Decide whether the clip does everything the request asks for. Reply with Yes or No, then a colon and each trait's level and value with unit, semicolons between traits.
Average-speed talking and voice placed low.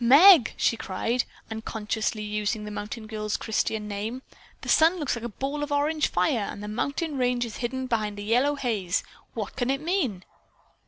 No: average, 190 wpm; high, 235 Hz